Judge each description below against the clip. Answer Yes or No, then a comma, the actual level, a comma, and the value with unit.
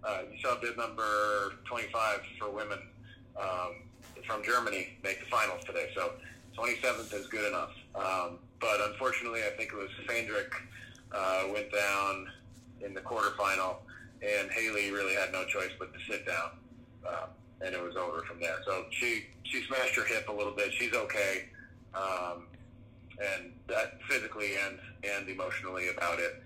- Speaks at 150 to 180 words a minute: Yes, average, 160 wpm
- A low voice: Yes, low, 105 Hz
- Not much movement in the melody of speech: No, average, 3.2 semitones